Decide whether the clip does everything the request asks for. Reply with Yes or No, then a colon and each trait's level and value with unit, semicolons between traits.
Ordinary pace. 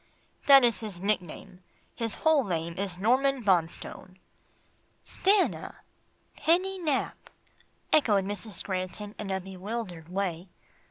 No: slow, 110 wpm